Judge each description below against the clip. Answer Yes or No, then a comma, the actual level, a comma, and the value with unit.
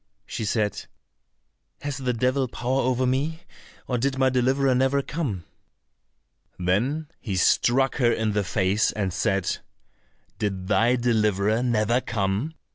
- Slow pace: Yes, slow, 130 wpm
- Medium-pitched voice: No, low, 120 Hz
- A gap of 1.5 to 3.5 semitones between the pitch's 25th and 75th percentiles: No, average, 4.2 semitones